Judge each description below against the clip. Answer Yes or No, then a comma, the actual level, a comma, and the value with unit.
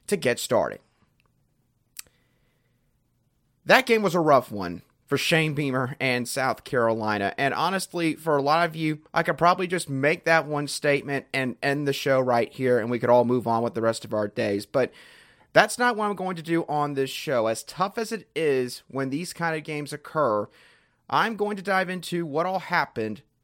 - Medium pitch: Yes, medium, 145 Hz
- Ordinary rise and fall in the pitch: No, wide, 5.7 semitones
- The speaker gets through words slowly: No, average, 200 wpm